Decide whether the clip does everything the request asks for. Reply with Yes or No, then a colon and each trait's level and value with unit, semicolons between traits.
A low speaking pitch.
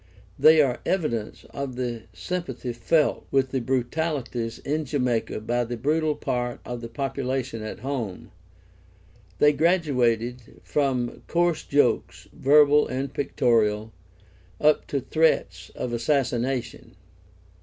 Yes: low, 130 Hz